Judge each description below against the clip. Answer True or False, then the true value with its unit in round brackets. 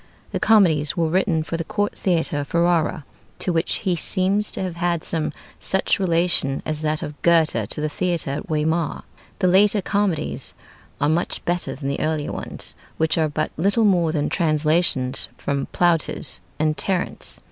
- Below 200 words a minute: True (170 wpm)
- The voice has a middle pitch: True (165 Hz)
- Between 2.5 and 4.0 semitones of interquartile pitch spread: True (3.0 semitones)